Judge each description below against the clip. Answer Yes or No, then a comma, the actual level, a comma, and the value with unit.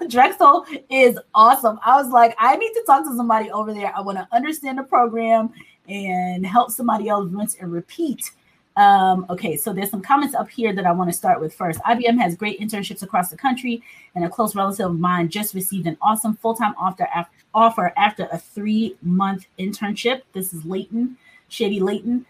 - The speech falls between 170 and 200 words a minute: Yes, average, 195 wpm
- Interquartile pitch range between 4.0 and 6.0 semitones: Yes, average, 4.3 semitones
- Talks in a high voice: Yes, high, 215 Hz